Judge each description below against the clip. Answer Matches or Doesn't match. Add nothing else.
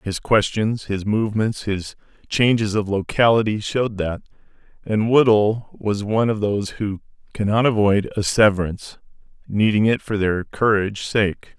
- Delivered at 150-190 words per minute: Doesn't match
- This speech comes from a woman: Doesn't match